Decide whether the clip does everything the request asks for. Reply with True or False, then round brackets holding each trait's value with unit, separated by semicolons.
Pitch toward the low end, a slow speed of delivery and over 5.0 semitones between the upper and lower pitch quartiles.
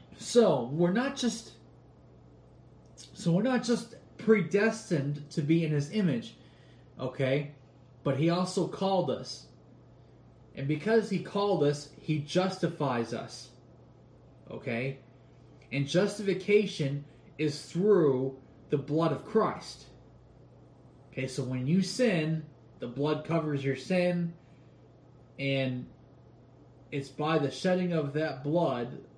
False (155 Hz; 115 wpm; 5.4 semitones)